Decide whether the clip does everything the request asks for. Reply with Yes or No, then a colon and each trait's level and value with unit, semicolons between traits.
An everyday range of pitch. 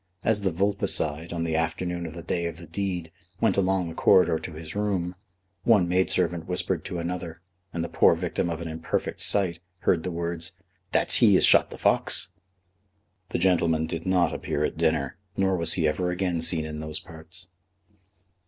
No: narrow, 2.0 semitones